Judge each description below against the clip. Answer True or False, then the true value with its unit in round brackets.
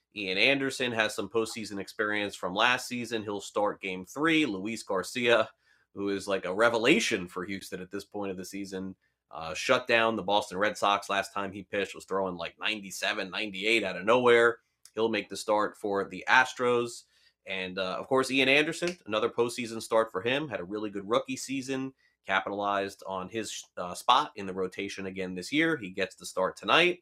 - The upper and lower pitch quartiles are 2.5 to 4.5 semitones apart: True (3.6 semitones)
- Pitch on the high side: False (105 Hz)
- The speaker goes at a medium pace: True (195 wpm)